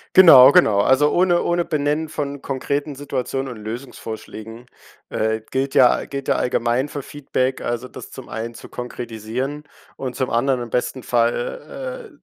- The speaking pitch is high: No, low, 130 Hz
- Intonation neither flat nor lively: Yes, average, 3.6 semitones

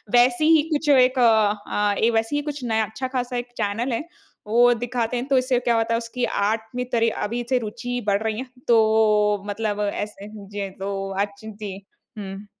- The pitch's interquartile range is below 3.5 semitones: Yes, average, 3.0 semitones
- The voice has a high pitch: Yes, high, 230 Hz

